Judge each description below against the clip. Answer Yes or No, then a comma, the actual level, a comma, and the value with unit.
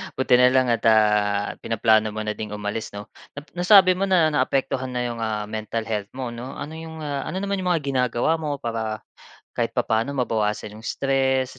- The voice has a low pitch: Yes, low, 125 Hz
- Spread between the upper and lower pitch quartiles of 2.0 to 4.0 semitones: No, average, 4.7 semitones